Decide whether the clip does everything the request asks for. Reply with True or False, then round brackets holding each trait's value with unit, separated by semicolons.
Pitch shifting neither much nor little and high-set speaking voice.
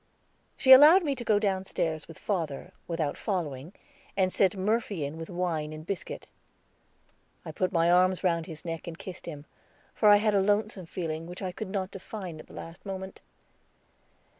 False (3.5 semitones; 180 Hz)